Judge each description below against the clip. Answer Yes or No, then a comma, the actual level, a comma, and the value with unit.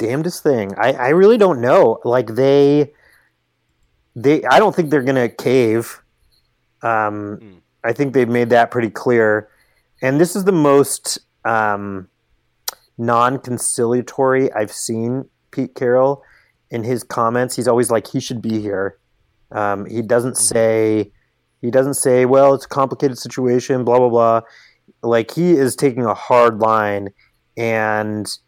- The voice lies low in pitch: Yes, low, 120 Hz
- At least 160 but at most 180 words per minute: No, average, 145 wpm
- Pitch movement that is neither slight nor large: Yes, average, 3.3 semitones